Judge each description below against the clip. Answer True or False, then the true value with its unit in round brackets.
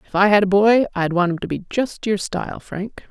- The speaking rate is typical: False (270 wpm)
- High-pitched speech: True (200 Hz)